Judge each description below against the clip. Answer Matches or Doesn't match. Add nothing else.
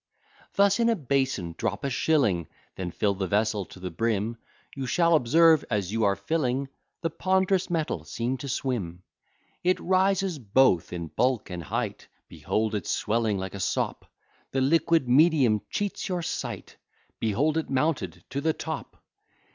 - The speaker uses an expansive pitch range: Matches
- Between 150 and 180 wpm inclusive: Matches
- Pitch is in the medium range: Doesn't match